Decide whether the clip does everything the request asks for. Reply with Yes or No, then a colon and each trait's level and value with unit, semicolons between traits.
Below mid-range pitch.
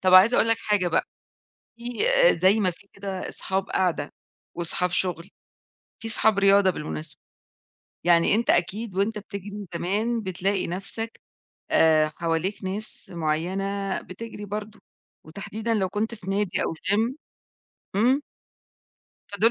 No: high, 195 Hz